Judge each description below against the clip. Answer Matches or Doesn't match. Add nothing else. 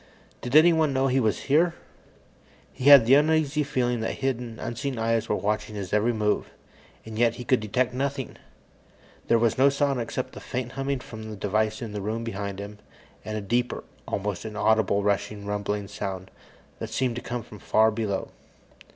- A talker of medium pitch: Doesn't match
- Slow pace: Doesn't match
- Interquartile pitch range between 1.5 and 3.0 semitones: Doesn't match